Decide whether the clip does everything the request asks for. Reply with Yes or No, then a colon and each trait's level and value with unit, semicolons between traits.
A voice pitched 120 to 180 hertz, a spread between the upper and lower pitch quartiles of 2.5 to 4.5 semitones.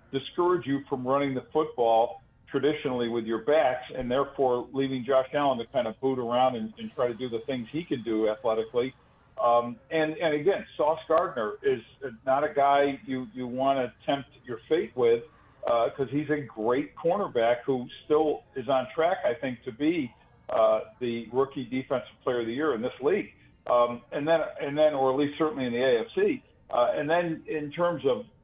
Yes: low, 135 Hz; average, 4.0 semitones